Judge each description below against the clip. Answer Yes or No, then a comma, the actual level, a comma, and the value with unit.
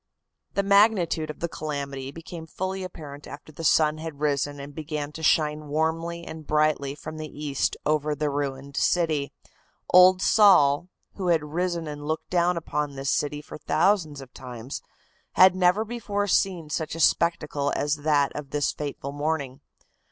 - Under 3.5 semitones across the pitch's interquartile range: Yes, average, 2.9 semitones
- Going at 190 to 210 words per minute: No, average, 165 wpm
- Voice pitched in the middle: Yes, medium, 155 Hz